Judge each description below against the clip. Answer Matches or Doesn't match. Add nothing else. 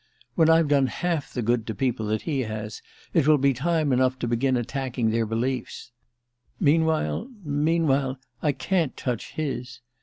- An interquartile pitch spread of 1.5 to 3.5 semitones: Doesn't match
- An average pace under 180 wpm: Matches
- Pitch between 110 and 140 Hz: Matches